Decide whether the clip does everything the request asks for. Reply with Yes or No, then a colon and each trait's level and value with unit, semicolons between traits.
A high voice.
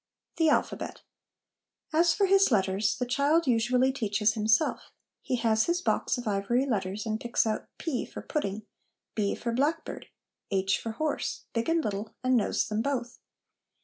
Yes: high, 235 Hz